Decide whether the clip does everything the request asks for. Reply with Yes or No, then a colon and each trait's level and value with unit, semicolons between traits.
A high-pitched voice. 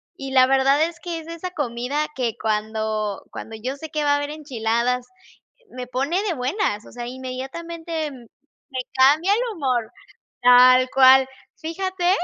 Yes: very high, 265 Hz